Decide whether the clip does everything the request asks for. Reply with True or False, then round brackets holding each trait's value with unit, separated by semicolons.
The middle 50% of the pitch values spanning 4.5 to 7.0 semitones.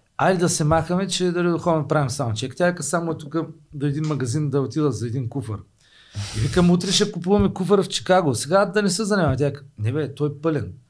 True (5.0 semitones)